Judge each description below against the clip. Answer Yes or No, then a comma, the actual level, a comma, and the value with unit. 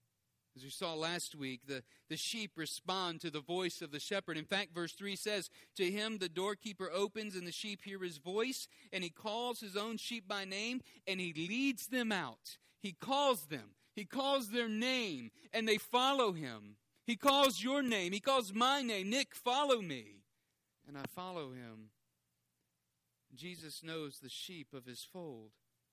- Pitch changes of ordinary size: No, wide, 7.5 semitones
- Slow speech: No, average, 180 wpm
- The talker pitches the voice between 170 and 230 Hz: Yes, medium, 185 Hz